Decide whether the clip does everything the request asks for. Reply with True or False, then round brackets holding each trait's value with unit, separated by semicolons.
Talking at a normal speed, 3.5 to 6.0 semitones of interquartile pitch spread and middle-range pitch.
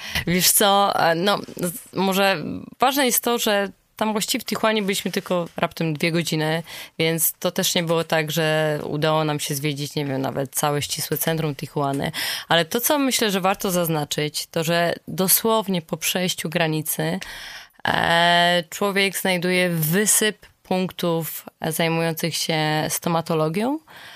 True (135 wpm; 3.9 semitones; 170 Hz)